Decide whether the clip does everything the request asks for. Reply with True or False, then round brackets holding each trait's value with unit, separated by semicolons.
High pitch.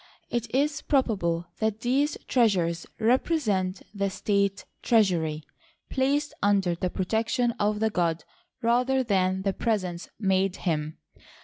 True (205 Hz)